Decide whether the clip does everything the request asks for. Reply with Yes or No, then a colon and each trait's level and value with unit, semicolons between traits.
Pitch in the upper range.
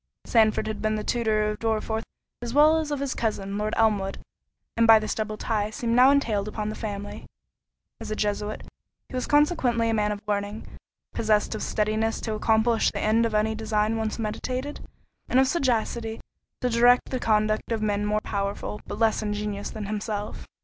Yes: high, 220 Hz